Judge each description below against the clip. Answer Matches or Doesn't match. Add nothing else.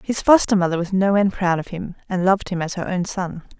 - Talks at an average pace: Doesn't match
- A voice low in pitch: Doesn't match